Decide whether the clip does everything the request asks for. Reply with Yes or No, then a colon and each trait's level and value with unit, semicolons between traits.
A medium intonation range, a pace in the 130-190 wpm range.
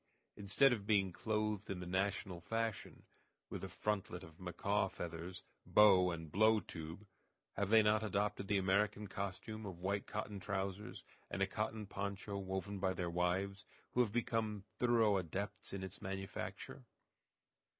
No: narrow, 2.2 semitones; average, 150 wpm